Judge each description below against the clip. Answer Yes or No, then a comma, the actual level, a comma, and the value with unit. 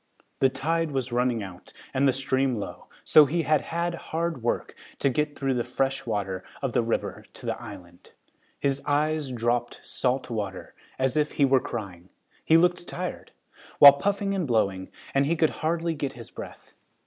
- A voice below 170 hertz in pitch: Yes, low, 135 Hz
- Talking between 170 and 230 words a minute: Yes, average, 185 wpm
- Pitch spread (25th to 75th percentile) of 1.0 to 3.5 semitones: No, average, 4.7 semitones